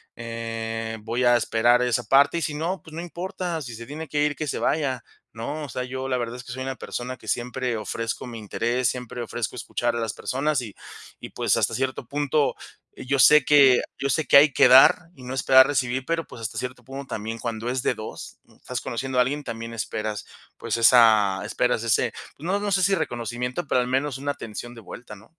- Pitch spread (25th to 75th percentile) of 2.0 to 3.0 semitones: No, average, 3.5 semitones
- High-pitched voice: No, low, 125 Hz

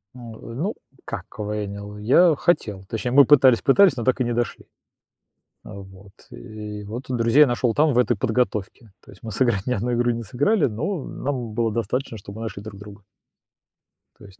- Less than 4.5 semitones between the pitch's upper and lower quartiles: Yes, average, 3.5 semitones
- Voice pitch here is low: Yes, low, 115 Hz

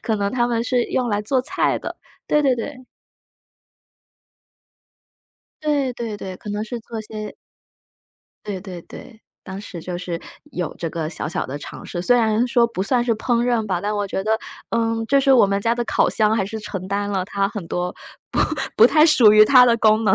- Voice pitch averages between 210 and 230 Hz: Yes, high, 220 Hz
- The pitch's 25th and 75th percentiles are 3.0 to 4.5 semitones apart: Yes, average, 3.4 semitones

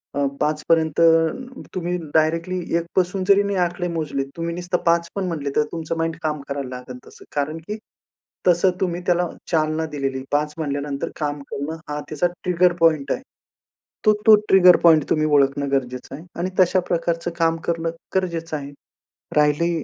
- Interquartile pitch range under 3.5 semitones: Yes, average, 3.0 semitones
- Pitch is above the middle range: No, medium, 165 Hz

